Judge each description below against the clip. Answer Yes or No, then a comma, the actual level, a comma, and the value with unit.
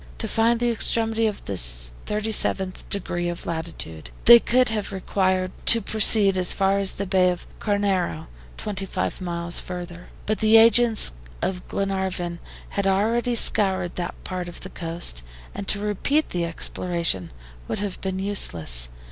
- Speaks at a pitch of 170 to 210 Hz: Yes, high, 190 Hz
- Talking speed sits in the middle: Yes, average, 150 wpm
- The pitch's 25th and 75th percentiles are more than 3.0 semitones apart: Yes, average, 3.4 semitones